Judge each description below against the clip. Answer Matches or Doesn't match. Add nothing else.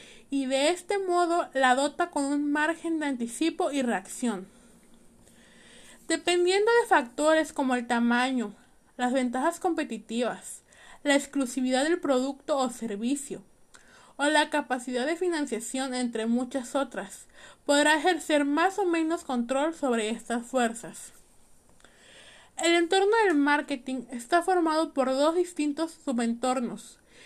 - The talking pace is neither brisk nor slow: Doesn't match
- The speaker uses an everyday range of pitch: Matches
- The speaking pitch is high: Matches